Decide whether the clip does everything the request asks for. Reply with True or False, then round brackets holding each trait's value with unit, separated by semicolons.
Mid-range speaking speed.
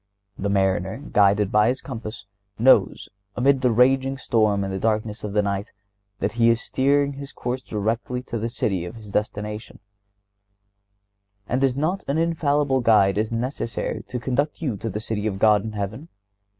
True (175 wpm)